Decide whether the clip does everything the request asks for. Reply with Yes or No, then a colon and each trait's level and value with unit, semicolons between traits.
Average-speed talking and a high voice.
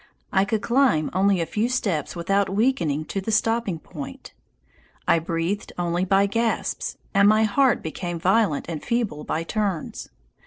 Yes: average, 155 wpm; high, 195 Hz